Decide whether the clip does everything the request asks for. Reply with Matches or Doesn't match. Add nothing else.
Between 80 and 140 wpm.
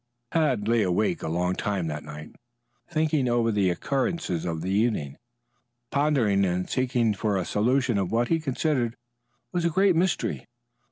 Doesn't match